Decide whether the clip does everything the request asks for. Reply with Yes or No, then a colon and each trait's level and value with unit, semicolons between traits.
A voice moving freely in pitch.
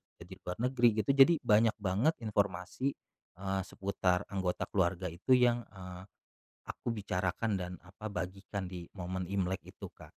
No: average, 2.7 semitones